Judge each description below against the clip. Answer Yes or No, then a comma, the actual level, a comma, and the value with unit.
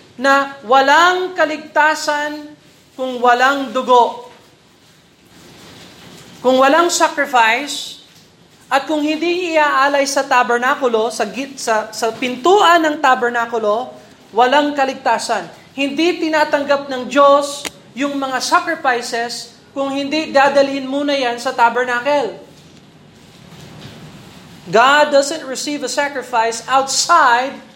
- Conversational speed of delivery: No, slow, 95 wpm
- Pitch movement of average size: Yes, average, 3.1 semitones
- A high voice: Yes, very high, 275 Hz